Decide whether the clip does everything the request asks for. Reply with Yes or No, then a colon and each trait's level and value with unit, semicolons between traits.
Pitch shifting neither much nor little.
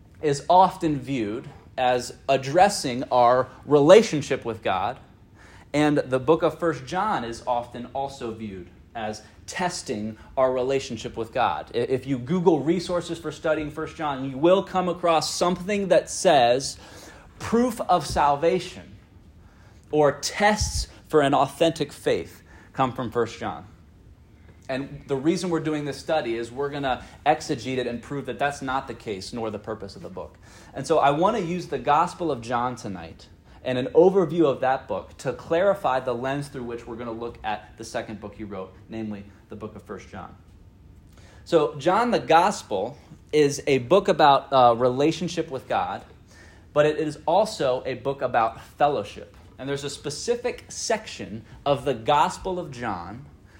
No: wide, 6.3 semitones